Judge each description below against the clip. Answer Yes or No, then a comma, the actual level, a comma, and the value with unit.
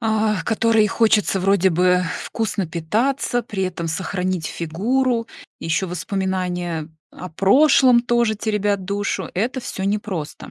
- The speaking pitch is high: Yes, high, 200 Hz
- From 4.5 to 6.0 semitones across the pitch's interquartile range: No, average, 3.7 semitones